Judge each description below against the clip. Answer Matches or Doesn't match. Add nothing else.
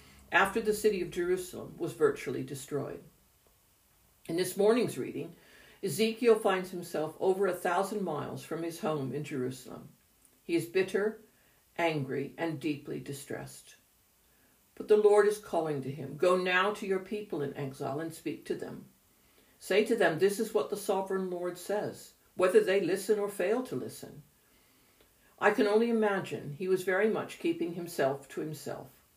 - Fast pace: Doesn't match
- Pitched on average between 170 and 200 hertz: Matches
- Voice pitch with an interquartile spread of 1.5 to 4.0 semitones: Doesn't match